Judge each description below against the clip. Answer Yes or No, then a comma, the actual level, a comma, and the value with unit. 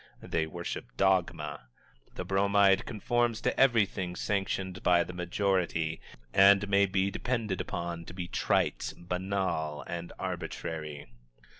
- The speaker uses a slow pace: Yes, slow, 120 wpm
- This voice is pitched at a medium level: No, very low, 95 Hz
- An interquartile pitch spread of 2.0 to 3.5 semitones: Yes, narrow, 2.6 semitones